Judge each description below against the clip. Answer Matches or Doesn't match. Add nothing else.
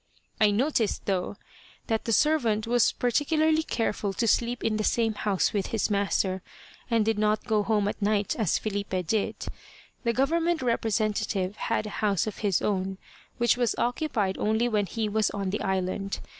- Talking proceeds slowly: Doesn't match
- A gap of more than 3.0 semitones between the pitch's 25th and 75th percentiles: Doesn't match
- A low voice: Doesn't match